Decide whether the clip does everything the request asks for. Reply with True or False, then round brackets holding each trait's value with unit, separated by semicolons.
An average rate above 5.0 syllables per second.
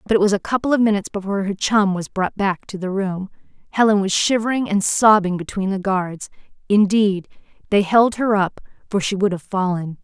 True (5.5 syllables/s)